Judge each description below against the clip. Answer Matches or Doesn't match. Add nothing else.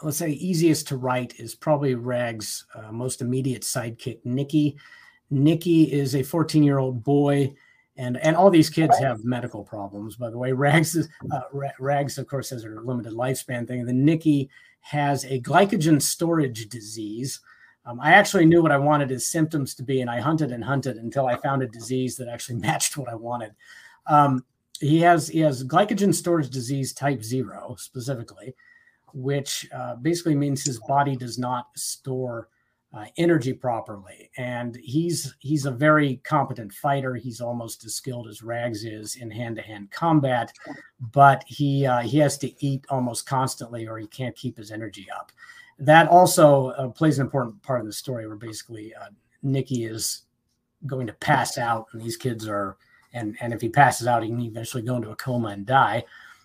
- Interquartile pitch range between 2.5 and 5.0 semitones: Matches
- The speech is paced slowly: Doesn't match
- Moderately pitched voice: Doesn't match